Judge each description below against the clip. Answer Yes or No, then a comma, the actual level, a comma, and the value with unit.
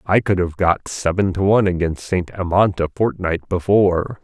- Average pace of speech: Yes, average, 185 wpm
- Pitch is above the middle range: No, very low, 90 Hz